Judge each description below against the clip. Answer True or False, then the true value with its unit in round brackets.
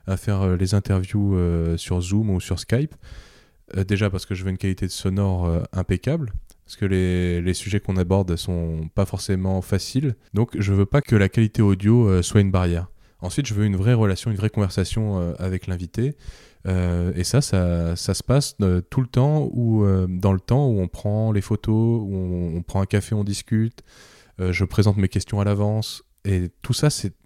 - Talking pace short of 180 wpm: False (195 wpm)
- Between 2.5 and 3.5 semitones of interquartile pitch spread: True (3.0 semitones)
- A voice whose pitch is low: True (100 Hz)